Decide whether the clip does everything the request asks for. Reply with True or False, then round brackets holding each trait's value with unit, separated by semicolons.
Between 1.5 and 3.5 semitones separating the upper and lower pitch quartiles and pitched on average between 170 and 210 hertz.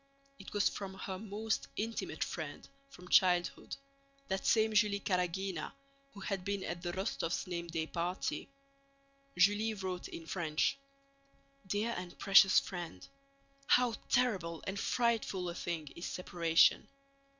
True (2.9 semitones; 190 Hz)